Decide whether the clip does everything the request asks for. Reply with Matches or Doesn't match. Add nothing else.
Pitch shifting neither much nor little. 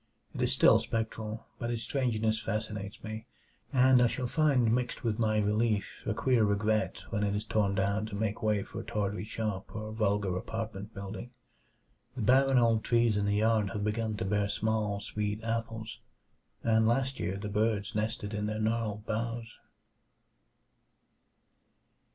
Doesn't match